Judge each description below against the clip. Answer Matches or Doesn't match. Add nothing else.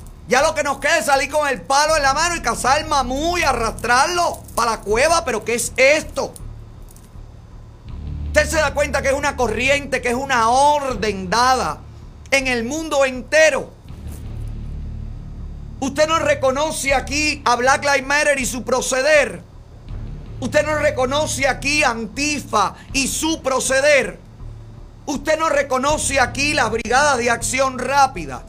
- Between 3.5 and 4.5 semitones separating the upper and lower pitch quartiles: Matches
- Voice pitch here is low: Doesn't match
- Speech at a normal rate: Matches